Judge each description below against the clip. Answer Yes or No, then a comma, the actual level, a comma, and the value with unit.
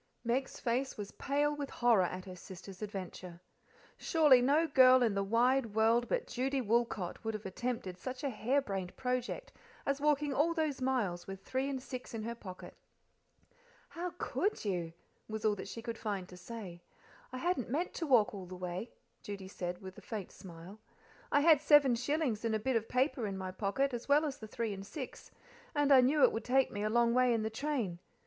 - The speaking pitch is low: No, high, 235 Hz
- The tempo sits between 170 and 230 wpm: Yes, average, 200 wpm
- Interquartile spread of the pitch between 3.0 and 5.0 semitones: No, wide, 5.4 semitones